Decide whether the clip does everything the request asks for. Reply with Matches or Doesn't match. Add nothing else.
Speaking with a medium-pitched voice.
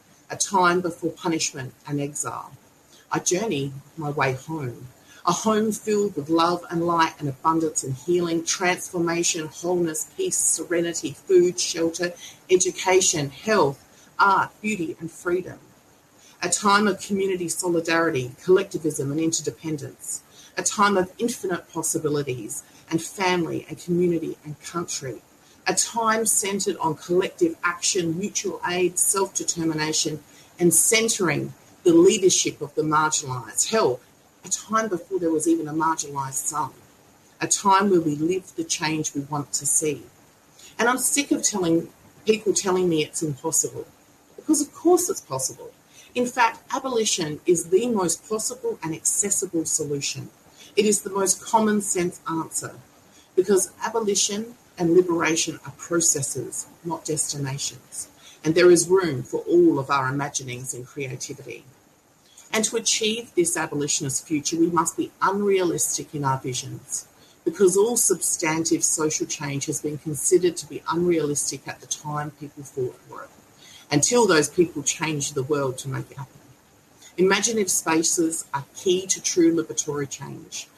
Matches